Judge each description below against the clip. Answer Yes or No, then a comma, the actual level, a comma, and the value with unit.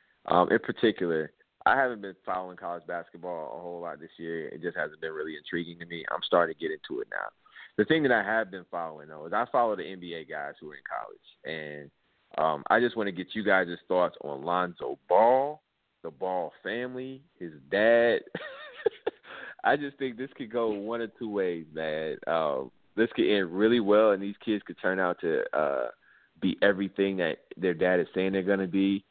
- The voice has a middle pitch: No, low, 100 Hz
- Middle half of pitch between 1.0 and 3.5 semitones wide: No, wide, 5.5 semitones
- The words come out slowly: No, fast, 205 wpm